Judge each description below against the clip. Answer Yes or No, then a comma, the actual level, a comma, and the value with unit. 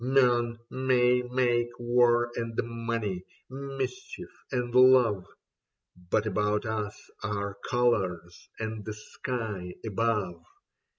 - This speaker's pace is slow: Yes, slow, 105 wpm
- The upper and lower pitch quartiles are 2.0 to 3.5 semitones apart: Yes, average, 2.9 semitones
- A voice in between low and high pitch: No, low, 115 Hz